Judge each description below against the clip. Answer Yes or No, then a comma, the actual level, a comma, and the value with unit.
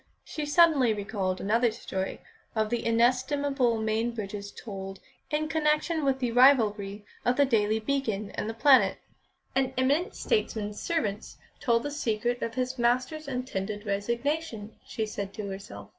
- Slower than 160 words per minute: Yes, average, 145 wpm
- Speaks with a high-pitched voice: Yes, high, 235 Hz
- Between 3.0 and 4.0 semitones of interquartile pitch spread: No, average, 4.5 semitones